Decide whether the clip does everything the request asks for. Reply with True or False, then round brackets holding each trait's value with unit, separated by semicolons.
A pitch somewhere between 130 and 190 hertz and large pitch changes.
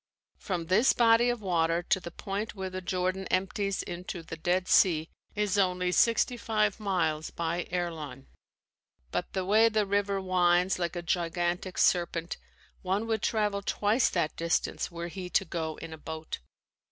False (185 Hz; 2.8 semitones)